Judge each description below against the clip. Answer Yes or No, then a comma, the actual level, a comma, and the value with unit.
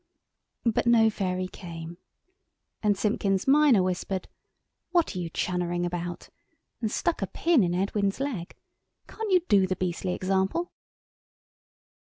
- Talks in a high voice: Yes, high, 195 Hz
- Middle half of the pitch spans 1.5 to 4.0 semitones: No, average, 4.5 semitones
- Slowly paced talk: Yes, slow, 130 wpm